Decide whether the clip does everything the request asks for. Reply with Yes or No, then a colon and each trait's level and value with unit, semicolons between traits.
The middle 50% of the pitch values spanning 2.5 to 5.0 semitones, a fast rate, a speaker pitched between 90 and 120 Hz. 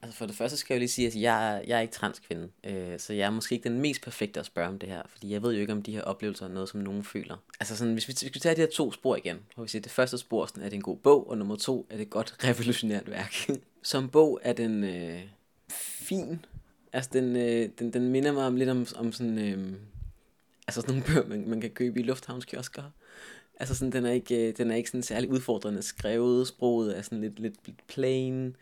Yes: average, 3.3 semitones; fast, 260 wpm; low, 115 Hz